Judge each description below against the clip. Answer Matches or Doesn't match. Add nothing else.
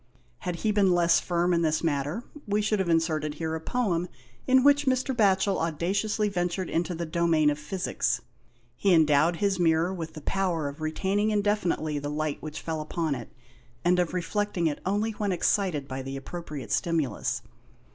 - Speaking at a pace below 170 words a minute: Doesn't match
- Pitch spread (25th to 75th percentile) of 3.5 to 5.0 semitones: Matches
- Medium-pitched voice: Matches